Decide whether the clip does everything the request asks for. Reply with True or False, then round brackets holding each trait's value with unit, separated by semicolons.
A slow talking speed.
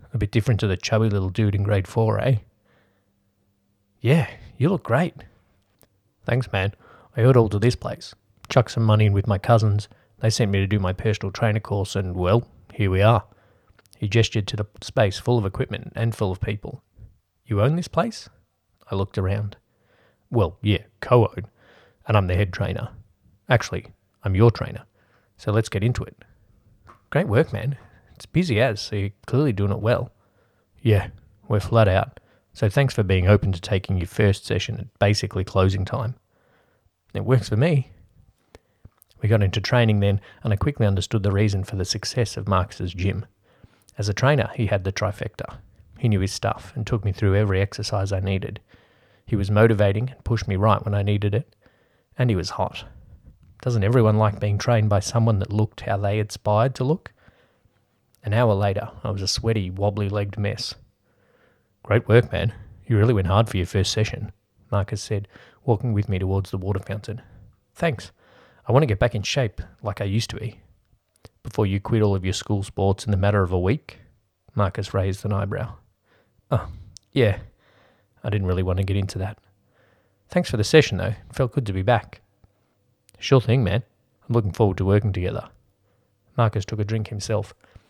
False (190 wpm)